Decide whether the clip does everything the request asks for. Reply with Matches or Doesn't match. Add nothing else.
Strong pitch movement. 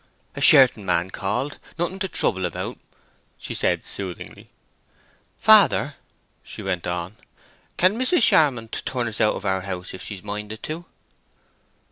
Matches